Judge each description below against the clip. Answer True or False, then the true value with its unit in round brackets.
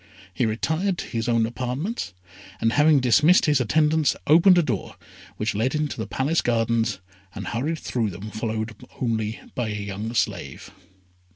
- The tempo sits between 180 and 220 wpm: False (160 wpm)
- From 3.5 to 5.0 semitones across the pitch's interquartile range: False (5.5 semitones)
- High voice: False (120 Hz)